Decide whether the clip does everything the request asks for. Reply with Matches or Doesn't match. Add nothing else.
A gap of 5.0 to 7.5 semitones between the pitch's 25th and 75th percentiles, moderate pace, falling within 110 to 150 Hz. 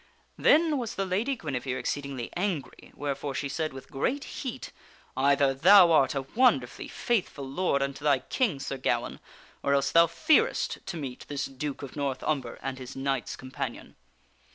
Matches